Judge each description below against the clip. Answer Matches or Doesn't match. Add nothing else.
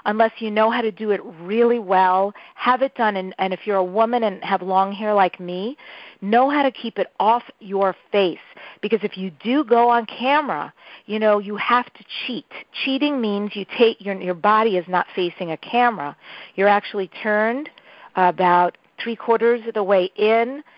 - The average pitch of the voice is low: Doesn't match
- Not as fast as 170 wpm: Doesn't match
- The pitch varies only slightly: Doesn't match